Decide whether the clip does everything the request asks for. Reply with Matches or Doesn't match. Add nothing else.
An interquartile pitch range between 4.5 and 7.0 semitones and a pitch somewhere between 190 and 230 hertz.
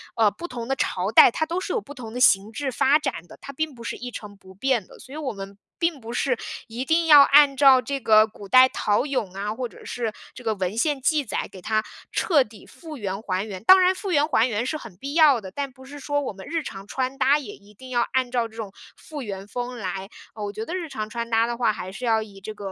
Doesn't match